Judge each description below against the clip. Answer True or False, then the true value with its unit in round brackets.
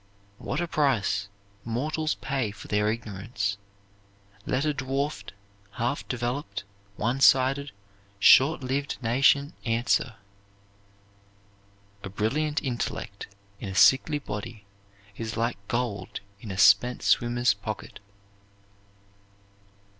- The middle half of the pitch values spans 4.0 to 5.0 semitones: True (4.6 semitones)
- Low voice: True (120 Hz)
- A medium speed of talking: False (100 wpm)